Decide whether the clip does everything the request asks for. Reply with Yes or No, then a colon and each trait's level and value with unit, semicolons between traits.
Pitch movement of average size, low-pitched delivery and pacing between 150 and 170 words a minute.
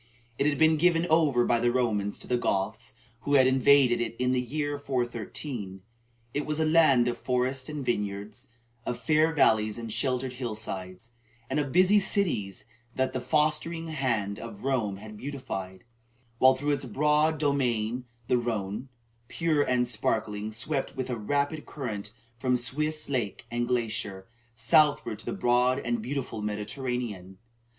Yes: average, 4.7 semitones; low, 125 Hz; average, 160 wpm